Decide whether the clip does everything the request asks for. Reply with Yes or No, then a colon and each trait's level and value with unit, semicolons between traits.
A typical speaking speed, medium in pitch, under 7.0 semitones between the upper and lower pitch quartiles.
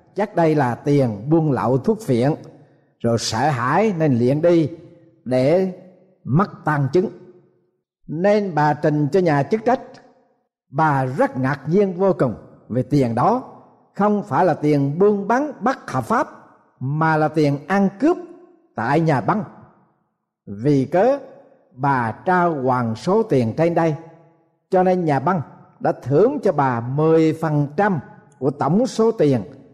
No: slow, 145 wpm; medium, 165 Hz; wide, 5.6 semitones